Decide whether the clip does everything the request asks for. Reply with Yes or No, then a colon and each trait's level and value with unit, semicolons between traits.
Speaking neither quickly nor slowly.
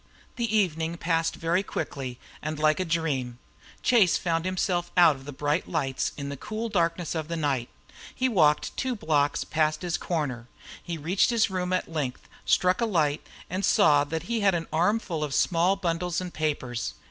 Yes: average, 180 wpm